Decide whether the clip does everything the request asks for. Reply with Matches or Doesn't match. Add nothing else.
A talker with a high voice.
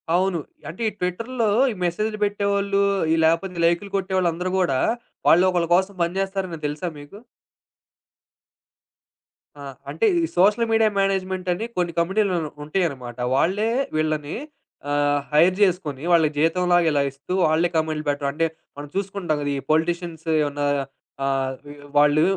Doesn't match